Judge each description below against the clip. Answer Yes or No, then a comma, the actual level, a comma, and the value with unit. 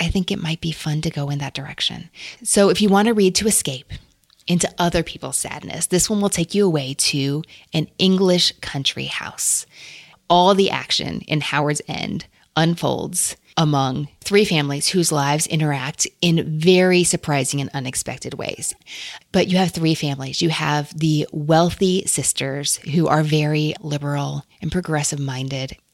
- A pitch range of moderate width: Yes, average, 3.7 semitones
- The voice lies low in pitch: No, medium, 160 Hz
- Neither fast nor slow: Yes, average, 160 wpm